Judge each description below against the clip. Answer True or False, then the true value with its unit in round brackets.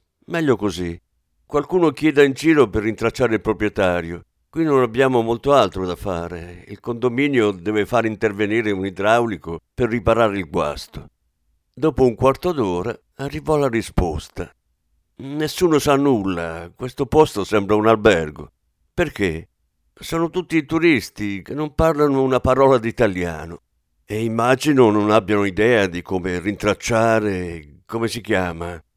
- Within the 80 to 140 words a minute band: True (135 wpm)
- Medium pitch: False (110 Hz)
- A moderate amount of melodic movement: False (7.1 semitones)